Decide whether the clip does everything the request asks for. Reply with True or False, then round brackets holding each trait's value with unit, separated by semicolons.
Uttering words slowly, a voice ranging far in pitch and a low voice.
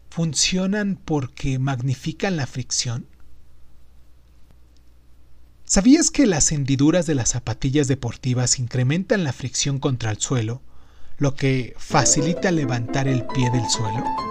True (115 wpm; 5.7 semitones; 130 Hz)